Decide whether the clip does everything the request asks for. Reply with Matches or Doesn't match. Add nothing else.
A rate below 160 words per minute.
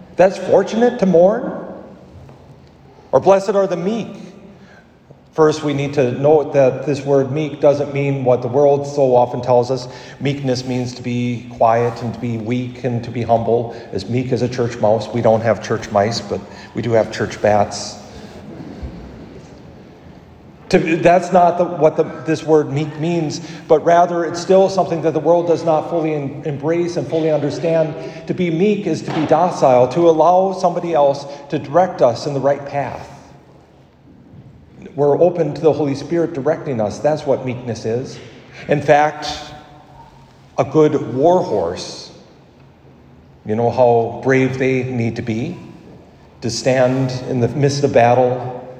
Doesn't match